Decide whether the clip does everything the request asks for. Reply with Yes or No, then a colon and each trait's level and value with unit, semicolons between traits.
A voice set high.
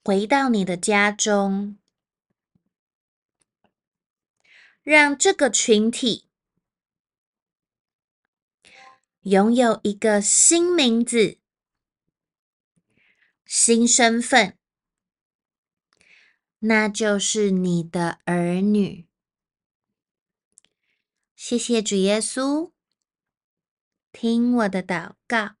Yes: high, 220 Hz